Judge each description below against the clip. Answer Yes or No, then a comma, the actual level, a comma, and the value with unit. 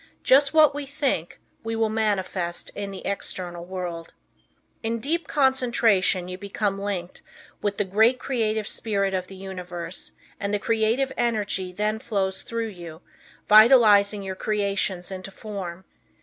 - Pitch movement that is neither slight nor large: Yes, average, 3.2 semitones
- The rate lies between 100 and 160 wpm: Yes, average, 140 wpm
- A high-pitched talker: Yes, high, 205 Hz